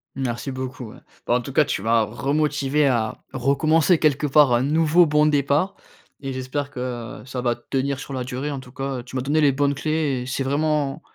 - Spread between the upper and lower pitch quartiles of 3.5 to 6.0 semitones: No, average, 2.7 semitones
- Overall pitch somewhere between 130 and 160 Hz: Yes, low, 135 Hz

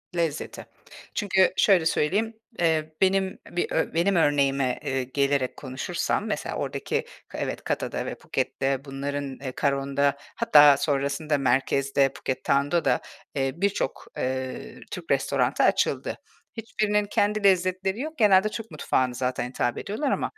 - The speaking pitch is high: No, medium, 145 Hz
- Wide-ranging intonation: Yes, wide, 5.9 semitones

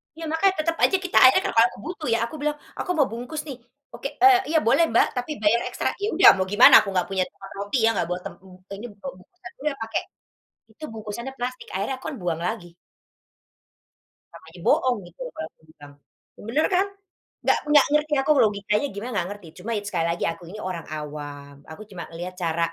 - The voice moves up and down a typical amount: No, wide, 8.4 semitones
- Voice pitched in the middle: No, high, 220 Hz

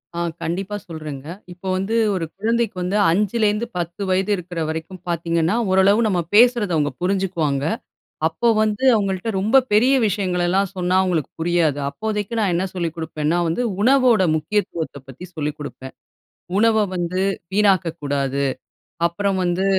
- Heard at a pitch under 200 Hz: Yes, medium, 185 Hz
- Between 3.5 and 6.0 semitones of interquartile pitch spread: Yes, average, 3.9 semitones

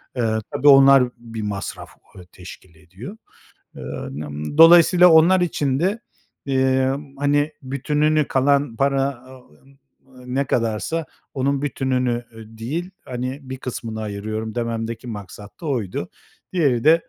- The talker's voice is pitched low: Yes, low, 130 Hz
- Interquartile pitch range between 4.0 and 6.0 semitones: Yes, average, 4.3 semitones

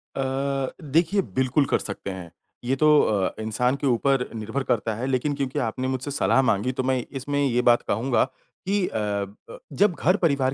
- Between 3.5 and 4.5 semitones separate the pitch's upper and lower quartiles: Yes, average, 3.9 semitones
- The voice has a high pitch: No, low, 130 Hz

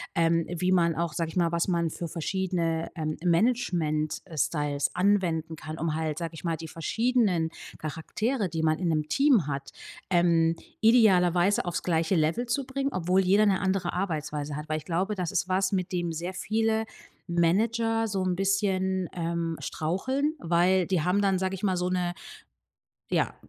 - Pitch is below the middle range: No, medium, 175 Hz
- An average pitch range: Yes, average, 3.0 semitones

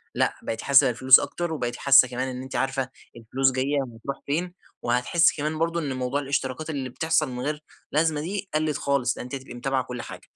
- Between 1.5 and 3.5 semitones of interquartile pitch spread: Yes, average, 3.2 semitones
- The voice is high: No, low, 135 Hz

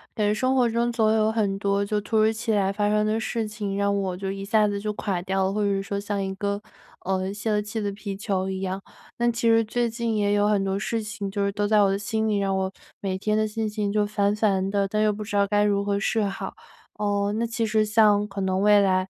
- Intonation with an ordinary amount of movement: No, narrow, 1.6 semitones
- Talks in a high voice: Yes, high, 205 Hz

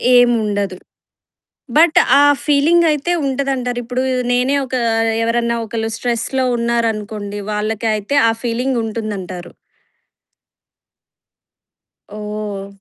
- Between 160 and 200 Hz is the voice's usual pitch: No, high, 230 Hz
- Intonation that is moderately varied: Yes, average, 3.2 semitones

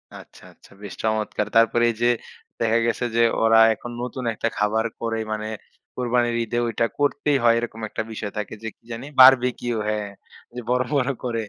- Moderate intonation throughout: No, narrow, 1.8 semitones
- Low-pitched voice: Yes, low, 115 Hz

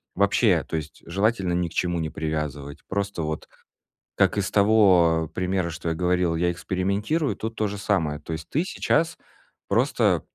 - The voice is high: No, very low, 90 Hz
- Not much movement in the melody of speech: No, average, 3.7 semitones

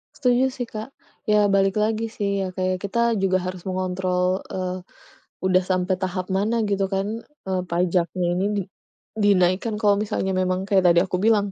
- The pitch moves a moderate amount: No, narrow, 2.3 semitones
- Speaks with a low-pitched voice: No, high, 190 Hz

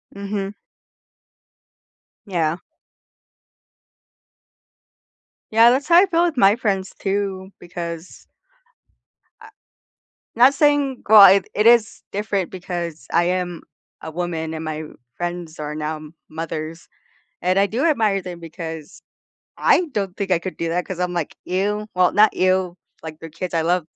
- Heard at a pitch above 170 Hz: Yes, medium, 185 Hz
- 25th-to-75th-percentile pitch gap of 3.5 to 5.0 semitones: Yes, average, 3.8 semitones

